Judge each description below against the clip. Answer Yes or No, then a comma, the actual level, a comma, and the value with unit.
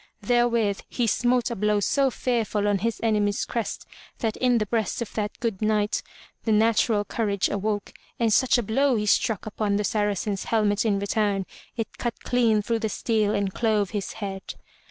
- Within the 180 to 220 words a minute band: Yes, average, 185 wpm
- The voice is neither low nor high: No, high, 215 Hz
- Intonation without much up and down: Yes, narrow, 2.0 semitones